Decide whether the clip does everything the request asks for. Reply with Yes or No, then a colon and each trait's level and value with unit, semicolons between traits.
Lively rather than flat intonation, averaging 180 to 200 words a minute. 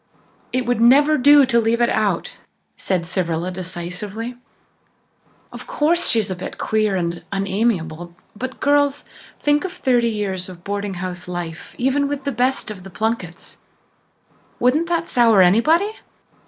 No: wide, 6.3 semitones; average, 140 wpm